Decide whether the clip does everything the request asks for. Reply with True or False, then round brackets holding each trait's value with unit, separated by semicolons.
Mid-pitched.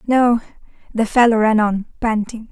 False (225 Hz)